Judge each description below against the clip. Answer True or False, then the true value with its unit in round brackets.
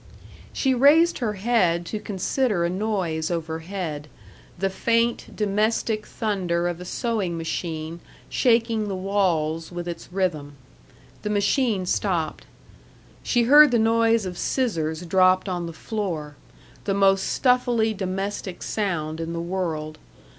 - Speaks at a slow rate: True (130 wpm)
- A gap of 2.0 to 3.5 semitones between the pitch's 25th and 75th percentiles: False (4.5 semitones)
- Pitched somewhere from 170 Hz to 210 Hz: True (190 Hz)